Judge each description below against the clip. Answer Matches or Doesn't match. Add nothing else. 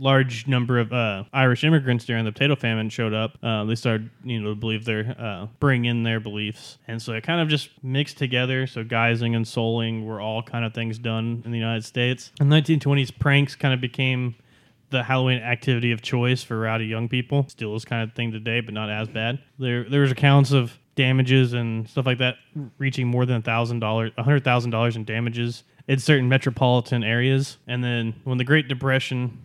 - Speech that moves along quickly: Matches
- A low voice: Matches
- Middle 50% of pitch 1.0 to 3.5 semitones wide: Matches